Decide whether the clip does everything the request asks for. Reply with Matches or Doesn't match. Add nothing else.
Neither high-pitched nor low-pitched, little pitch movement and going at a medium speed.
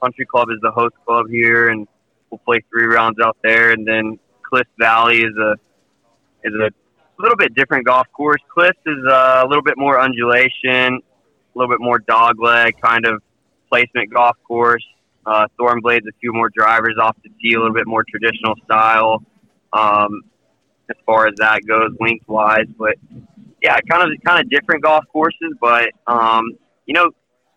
Doesn't match